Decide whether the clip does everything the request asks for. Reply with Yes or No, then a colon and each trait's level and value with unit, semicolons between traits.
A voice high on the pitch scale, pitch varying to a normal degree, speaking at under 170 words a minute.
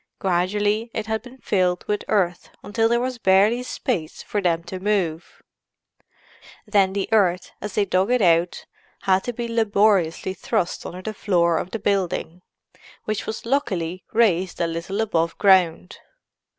Yes: high, 195 Hz; average, 3.5 semitones; average, 155 wpm